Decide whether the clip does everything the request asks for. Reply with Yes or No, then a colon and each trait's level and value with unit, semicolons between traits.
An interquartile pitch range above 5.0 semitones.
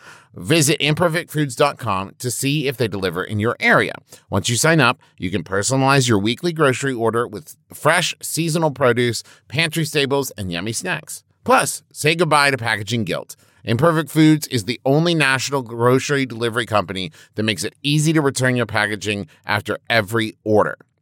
Yes: wide, 5.4 semitones